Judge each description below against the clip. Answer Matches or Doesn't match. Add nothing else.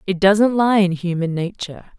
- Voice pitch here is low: Doesn't match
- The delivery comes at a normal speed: Matches